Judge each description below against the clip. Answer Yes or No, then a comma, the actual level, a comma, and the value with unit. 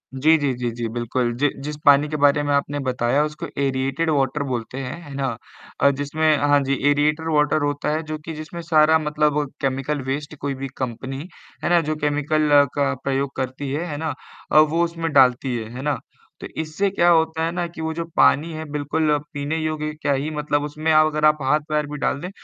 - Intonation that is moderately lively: No, narrow, 2.1 semitones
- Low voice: No, medium, 150 Hz